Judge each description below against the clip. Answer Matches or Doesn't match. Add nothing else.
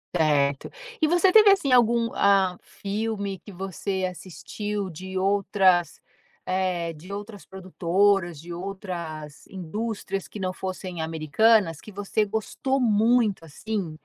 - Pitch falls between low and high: Doesn't match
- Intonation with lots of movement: Doesn't match